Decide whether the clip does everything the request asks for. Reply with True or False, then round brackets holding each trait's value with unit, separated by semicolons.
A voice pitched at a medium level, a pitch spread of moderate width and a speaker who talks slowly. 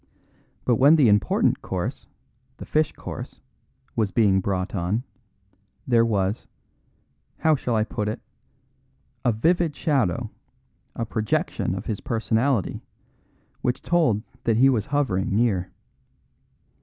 False (115 Hz; 4.5 semitones; 120 wpm)